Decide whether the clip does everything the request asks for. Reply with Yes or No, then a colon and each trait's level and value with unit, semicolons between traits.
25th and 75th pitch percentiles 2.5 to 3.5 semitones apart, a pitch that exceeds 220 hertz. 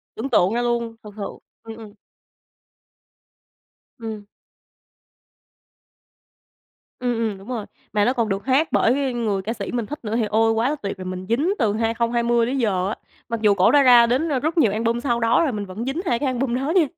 Yes: average, 2.9 semitones; high, 230 Hz